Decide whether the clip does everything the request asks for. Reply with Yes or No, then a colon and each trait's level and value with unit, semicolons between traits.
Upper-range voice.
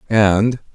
No: low, 105 Hz